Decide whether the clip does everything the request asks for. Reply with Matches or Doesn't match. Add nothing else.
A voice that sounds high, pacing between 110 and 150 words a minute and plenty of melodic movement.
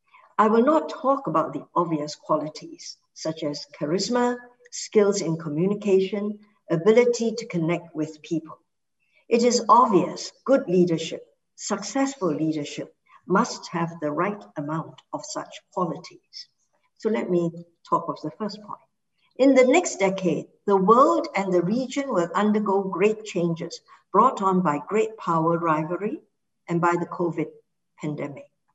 Matches